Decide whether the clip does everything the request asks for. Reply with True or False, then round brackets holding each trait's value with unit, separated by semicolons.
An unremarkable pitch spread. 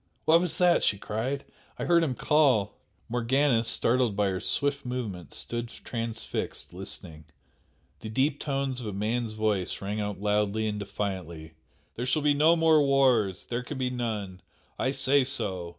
True (4.9 semitones)